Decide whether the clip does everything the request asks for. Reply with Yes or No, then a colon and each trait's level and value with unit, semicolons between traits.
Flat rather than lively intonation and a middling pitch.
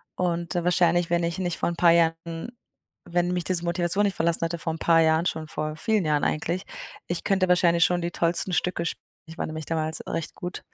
Yes: narrow, 1.4 semitones; medium, 170 Hz